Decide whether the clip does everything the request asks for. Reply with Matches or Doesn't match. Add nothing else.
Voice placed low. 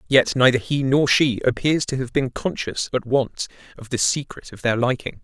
Matches